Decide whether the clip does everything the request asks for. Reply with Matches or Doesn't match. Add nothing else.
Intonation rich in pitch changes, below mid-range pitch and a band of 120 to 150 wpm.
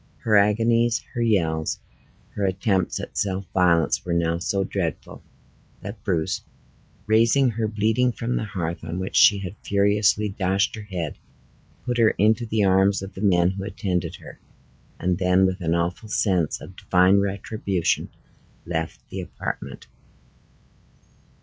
Doesn't match